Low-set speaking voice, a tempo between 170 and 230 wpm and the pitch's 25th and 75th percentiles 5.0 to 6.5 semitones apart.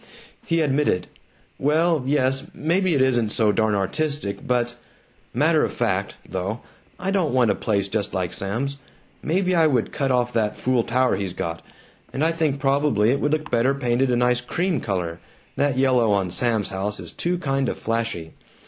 Yes: low, 125 Hz; average, 180 wpm; wide, 5.5 semitones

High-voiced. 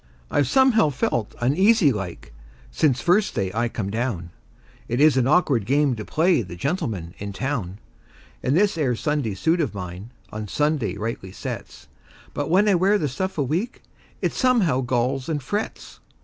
No: low, 135 Hz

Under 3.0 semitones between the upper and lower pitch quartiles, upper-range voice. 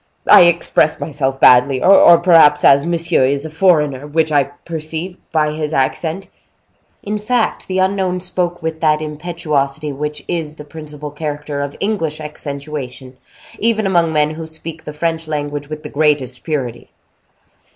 No: narrow, 2.5 semitones; medium, 155 Hz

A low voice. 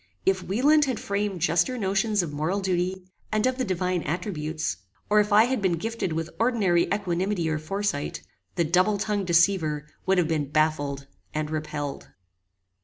No: medium, 185 Hz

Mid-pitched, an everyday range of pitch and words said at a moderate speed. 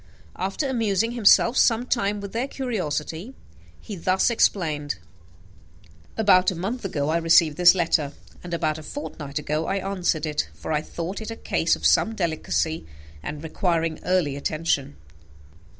Yes: medium, 175 Hz; average, 4.9 semitones; average, 150 wpm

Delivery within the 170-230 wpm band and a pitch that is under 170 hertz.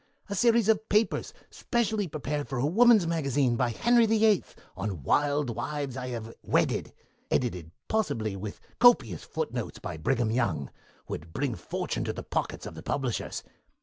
No: average, 155 wpm; medium, 140 Hz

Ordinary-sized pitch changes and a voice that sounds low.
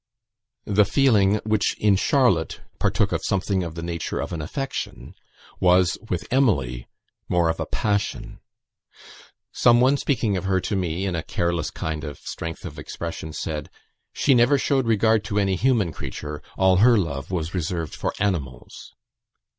Yes: average, 4.9 semitones; very low, 95 Hz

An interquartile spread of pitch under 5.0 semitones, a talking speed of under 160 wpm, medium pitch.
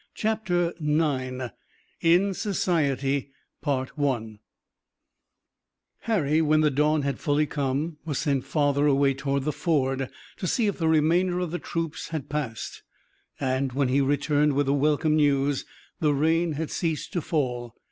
Yes: average, 2.9 semitones; average, 140 wpm; medium, 150 Hz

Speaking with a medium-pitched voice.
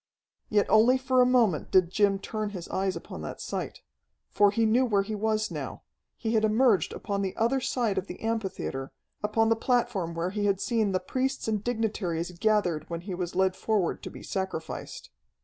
No: high, 210 Hz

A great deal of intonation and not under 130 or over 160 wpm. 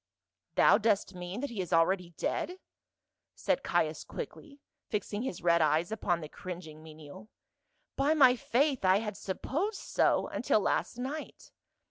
Yes: wide, 6.8 semitones; average, 150 wpm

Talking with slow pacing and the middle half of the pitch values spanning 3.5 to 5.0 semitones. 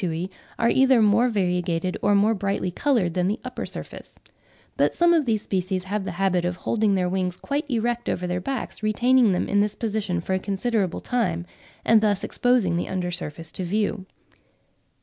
No: average, 195 wpm; average, 4.1 semitones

